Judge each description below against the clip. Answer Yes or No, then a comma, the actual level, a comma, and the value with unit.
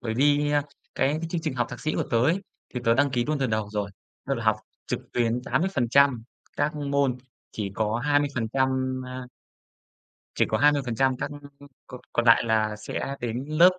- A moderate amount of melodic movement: Yes, average, 3.8 semitones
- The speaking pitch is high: No, low, 130 Hz